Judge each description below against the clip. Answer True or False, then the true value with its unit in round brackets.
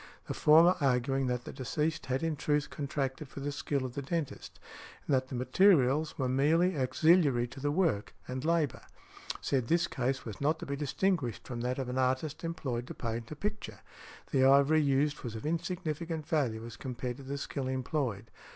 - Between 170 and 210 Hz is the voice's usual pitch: False (140 Hz)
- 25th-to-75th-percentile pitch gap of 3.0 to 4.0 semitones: True (3.5 semitones)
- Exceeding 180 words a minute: True (190 wpm)